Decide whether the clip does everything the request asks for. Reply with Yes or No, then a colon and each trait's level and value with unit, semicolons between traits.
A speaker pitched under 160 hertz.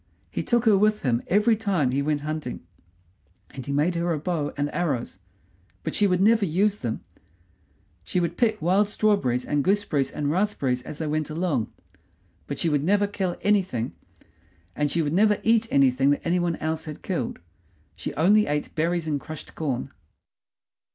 No: medium, 165 Hz